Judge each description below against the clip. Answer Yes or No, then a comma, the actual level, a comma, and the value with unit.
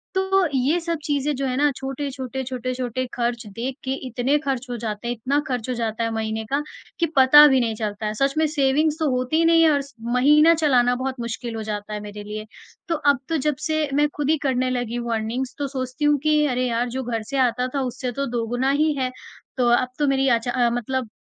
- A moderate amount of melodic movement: Yes, average, 3.2 semitones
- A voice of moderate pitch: No, very high, 255 Hz